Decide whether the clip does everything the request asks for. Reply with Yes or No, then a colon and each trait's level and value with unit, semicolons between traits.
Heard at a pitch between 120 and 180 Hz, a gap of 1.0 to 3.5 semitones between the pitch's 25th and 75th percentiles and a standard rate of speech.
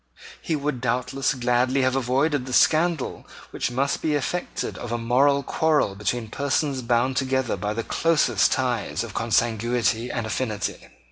Yes: low, 130 Hz; average, 3.0 semitones; average, 155 wpm